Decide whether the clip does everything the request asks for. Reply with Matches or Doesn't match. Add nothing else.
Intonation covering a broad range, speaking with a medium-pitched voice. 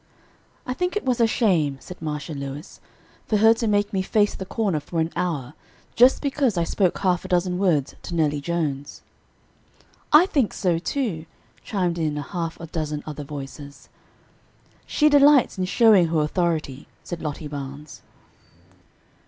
Matches